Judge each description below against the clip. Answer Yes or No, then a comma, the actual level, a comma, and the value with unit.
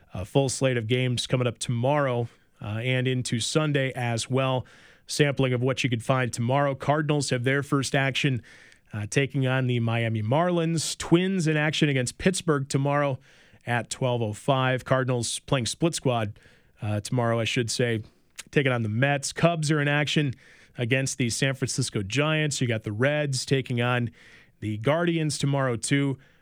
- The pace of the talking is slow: No, average, 165 wpm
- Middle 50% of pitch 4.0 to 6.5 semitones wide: No, average, 3.0 semitones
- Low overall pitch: Yes, low, 130 Hz